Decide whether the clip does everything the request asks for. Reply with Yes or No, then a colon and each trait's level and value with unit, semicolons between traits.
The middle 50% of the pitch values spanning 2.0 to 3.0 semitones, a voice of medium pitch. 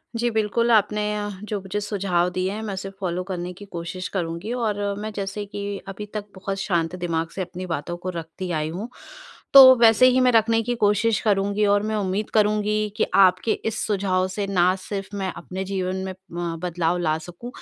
No: average, 2.7 semitones; high, 195 Hz